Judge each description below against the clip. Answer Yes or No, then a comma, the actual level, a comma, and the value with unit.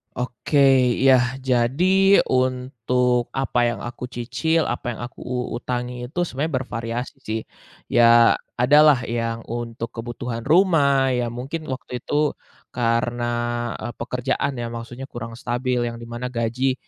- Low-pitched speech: Yes, low, 125 Hz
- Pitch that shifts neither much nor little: No, narrow, 2.0 semitones